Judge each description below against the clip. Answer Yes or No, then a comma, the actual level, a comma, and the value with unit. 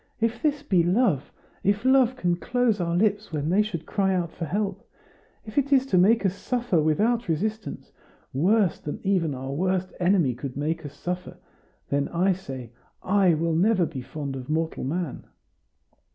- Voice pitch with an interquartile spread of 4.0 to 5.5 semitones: Yes, average, 5.2 semitones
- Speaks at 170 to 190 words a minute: Yes, average, 175 wpm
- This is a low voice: No, medium, 180 Hz